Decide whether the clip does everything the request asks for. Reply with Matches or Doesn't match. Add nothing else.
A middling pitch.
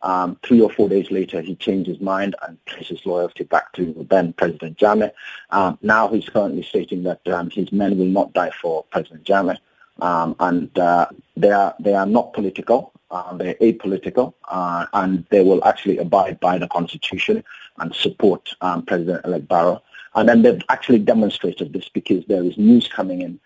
Doesn't match